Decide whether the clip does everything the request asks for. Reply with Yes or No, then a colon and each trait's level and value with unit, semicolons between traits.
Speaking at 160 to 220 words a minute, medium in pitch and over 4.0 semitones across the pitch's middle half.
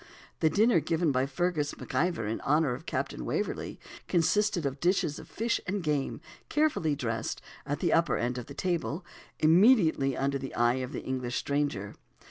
Yes: average, 170 wpm; medium, 150 Hz; average, 4.8 semitones